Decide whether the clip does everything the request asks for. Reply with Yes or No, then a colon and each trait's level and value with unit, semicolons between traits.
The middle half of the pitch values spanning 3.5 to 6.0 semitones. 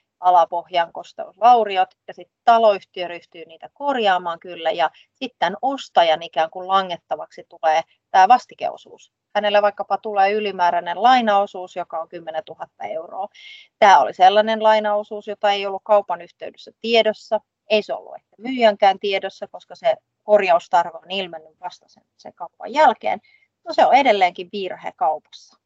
Yes: average, 3.9 semitones